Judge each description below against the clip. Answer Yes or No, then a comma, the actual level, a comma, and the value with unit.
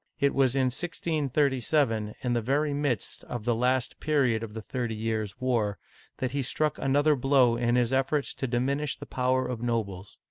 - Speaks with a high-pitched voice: No, low, 125 Hz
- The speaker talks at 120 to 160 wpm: No, average, 180 wpm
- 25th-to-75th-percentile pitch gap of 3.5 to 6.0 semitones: No, average, 3.1 semitones